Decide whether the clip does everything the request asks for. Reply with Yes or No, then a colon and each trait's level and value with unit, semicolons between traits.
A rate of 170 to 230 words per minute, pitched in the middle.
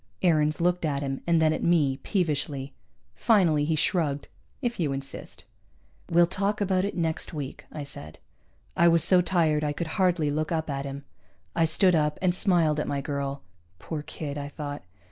Yes: average, 185 wpm; medium, 155 Hz